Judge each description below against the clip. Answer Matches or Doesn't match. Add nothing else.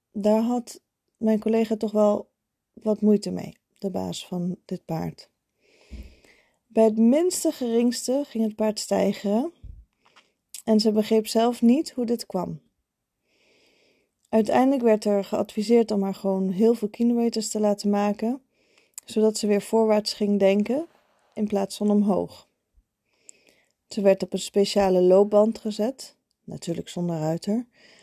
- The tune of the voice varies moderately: Doesn't match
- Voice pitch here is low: Doesn't match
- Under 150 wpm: Matches